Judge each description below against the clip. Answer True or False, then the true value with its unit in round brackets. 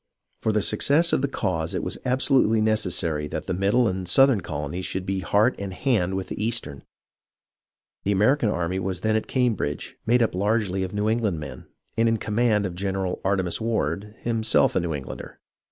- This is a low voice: True (100 Hz)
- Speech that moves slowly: False (195 wpm)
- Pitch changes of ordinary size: True (3.7 semitones)